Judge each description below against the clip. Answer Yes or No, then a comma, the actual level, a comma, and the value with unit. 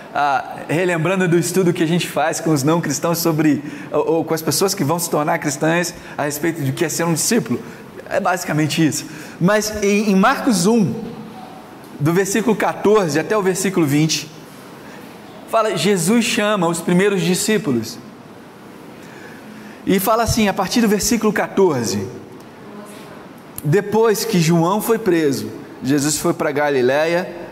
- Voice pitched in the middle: Yes, medium, 170 Hz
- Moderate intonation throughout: Yes, average, 4.6 semitones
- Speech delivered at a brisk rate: No, average, 145 wpm